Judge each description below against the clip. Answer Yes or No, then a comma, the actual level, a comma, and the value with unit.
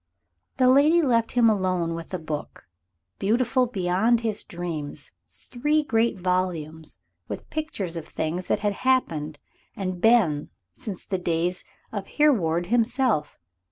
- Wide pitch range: Yes, wide, 6.2 semitones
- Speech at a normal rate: No, slow, 130 wpm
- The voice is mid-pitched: No, high, 195 Hz